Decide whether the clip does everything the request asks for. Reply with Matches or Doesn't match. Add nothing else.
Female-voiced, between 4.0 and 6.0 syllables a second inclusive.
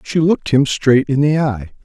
Doesn't match